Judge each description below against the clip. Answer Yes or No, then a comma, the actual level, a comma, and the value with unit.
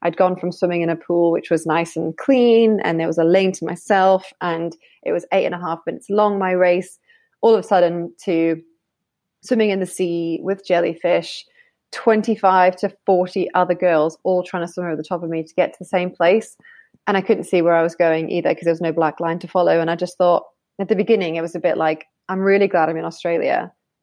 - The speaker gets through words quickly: Yes, fast, 240 wpm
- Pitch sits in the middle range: Yes, medium, 180 Hz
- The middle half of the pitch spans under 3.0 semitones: Yes, narrow, 2.5 semitones